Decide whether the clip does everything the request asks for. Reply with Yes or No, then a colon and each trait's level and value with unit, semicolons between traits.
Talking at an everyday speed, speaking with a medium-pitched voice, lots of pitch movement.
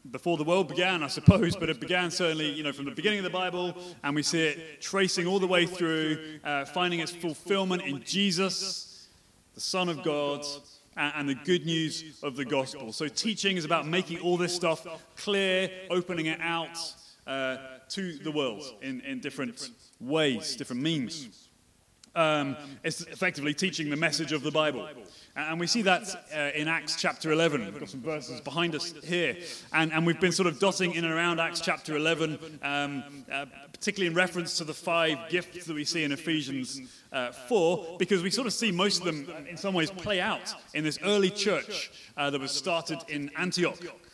No: average, 195 wpm; medium, 165 Hz; average, 3.3 semitones